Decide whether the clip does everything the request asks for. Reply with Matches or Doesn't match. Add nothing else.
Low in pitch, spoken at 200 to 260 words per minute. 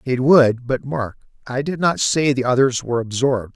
Matches